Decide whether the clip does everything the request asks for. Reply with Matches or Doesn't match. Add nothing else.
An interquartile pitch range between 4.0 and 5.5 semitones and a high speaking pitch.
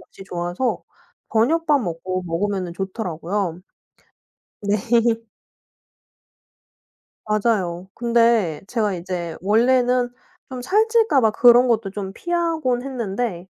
Matches